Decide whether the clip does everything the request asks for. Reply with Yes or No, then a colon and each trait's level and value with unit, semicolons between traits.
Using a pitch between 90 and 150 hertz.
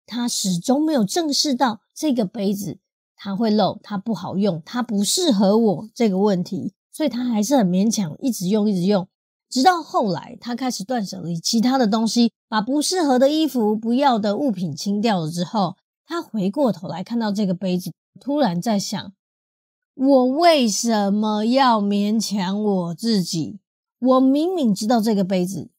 No: high, 220 Hz